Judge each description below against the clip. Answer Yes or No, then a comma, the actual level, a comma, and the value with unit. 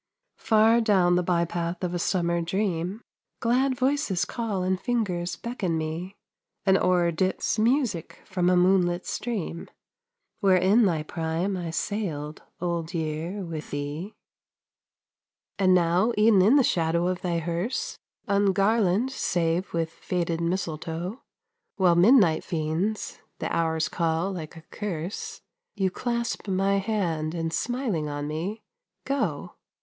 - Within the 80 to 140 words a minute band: Yes, slow, 135 wpm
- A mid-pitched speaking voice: Yes, medium, 180 Hz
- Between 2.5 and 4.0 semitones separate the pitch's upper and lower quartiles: Yes, average, 3.7 semitones